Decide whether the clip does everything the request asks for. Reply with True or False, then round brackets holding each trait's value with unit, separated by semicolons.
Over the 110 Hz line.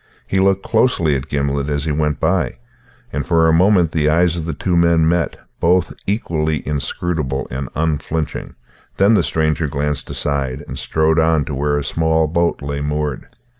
False (80 Hz)